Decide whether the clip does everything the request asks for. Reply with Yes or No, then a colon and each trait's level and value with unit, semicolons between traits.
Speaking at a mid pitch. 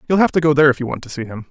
Yes: medium, 145 Hz